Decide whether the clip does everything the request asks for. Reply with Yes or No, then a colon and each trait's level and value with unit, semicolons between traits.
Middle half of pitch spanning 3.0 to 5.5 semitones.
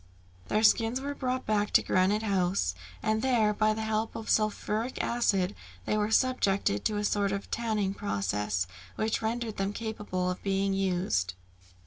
No: narrow, 2.4 semitones